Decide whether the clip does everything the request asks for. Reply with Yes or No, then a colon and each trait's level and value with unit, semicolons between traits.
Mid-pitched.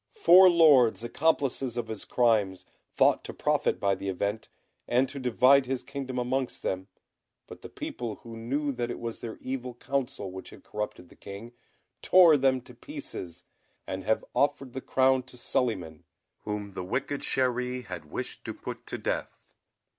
No: low, 125 Hz